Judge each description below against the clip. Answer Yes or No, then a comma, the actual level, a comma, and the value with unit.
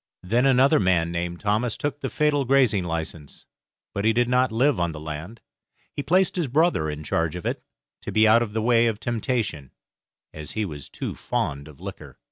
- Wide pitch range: Yes, wide, 7.2 semitones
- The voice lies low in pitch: Yes, low, 110 Hz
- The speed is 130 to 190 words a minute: No, average, 200 wpm